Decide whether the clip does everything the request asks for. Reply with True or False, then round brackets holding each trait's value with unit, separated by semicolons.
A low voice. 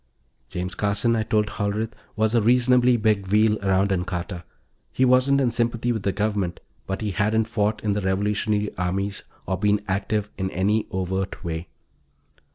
True (105 Hz)